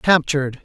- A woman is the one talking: No, male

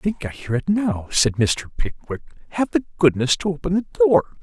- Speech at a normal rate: No, fast, 215 wpm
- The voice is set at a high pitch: No, medium, 165 Hz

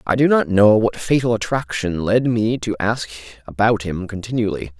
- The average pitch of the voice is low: Yes, low, 105 Hz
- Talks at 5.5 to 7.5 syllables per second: No, 5.0 syllables/s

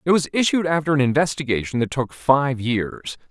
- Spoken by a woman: No, male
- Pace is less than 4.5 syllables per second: No, 5.2 syllables/s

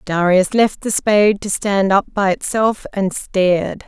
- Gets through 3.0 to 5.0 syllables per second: Yes, 4.1 syllables/s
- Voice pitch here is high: Yes, high, 200 Hz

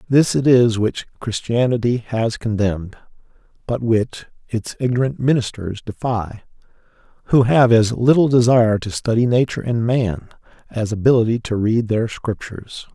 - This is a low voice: Yes, low, 115 Hz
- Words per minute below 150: Yes, slow, 135 wpm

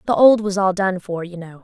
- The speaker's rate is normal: No, fast, 295 wpm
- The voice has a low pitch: No, high, 190 Hz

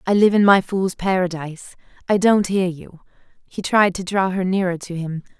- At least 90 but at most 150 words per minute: No, average, 200 wpm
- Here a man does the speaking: No, female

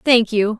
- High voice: Yes, high, 225 Hz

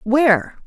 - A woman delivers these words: Yes, female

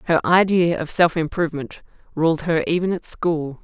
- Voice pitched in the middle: Yes, medium, 165 Hz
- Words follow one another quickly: No, average, 165 wpm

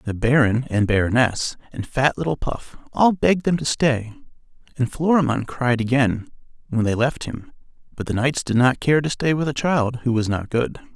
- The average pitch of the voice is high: No, low, 130 Hz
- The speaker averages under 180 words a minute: No, average, 195 wpm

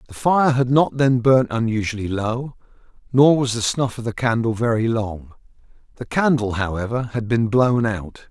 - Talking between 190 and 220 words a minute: No, average, 175 wpm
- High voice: No, low, 120 Hz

